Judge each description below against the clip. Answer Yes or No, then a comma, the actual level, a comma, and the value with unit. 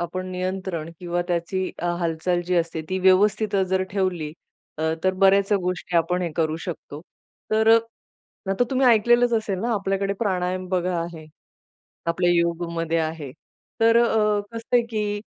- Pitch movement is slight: No, average, 3.3 semitones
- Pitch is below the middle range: No, medium, 185 Hz